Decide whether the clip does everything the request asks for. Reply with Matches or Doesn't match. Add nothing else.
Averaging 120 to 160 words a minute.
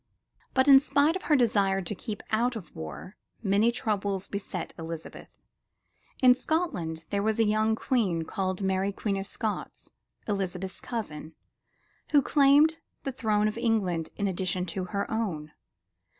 Matches